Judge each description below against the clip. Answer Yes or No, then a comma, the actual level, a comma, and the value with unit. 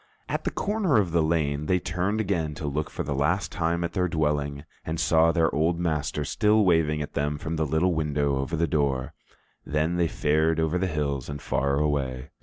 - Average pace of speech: No, fast, 210 wpm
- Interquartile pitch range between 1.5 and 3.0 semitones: Yes, average, 2.7 semitones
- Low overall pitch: Yes, very low, 80 Hz